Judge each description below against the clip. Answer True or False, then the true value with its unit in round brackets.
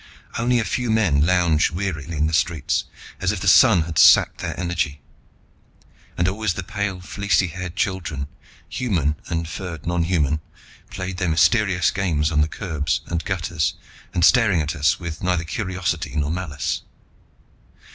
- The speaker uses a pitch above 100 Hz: False (90 Hz)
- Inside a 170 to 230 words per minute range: False (155 wpm)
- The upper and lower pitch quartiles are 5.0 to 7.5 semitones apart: False (3.2 semitones)